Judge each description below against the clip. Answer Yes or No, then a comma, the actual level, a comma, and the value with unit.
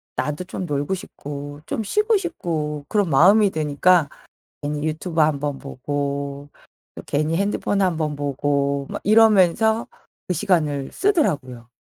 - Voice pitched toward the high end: No, medium, 155 Hz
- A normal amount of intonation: Yes, average, 5.0 semitones